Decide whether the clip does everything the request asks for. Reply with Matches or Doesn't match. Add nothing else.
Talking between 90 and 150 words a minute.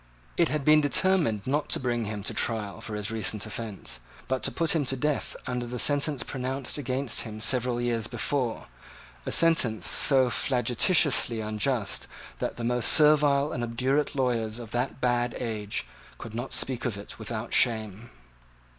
Doesn't match